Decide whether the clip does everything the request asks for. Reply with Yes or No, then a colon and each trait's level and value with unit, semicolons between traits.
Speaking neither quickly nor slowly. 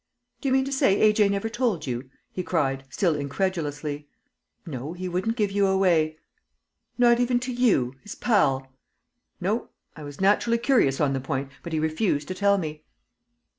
Yes: average, 170 wpm